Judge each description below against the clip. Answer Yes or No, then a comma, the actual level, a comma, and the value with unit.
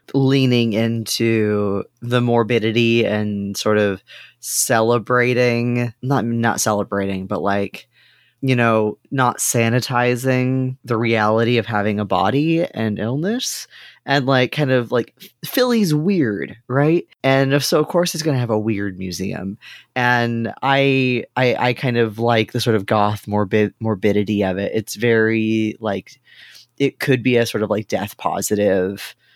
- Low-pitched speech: Yes, low, 115 Hz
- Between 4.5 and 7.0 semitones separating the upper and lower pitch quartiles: No, average, 3.3 semitones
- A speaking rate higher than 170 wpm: No, average, 145 wpm